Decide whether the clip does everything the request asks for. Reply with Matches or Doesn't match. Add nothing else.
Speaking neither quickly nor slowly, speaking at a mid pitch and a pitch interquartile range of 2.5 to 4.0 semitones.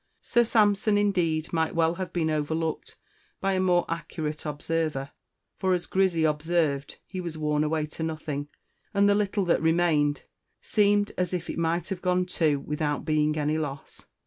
Matches